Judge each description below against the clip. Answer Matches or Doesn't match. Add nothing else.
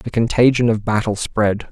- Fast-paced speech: Doesn't match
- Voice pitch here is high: Doesn't match